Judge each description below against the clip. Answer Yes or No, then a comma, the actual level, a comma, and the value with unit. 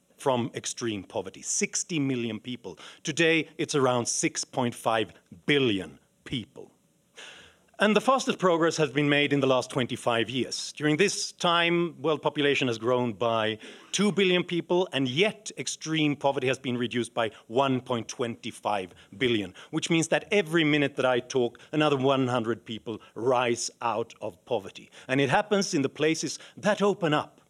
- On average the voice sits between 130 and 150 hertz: Yes, medium, 140 Hz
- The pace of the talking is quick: No, average, 150 wpm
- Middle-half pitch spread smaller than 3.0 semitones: No, average, 5.3 semitones